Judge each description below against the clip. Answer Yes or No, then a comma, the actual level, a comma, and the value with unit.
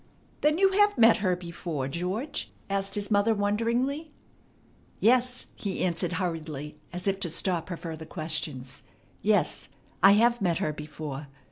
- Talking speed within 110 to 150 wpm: Yes, average, 145 wpm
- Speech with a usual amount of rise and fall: No, wide, 5.9 semitones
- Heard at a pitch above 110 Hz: Yes, medium, 185 Hz